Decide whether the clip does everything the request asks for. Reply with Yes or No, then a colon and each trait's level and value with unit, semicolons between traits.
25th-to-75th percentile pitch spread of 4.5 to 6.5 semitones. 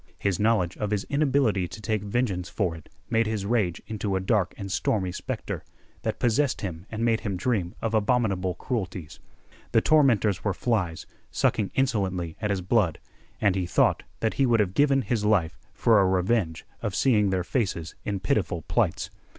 No: average, 3.7 semitones